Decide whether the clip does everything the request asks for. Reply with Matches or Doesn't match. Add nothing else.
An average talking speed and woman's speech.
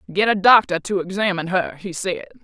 Matches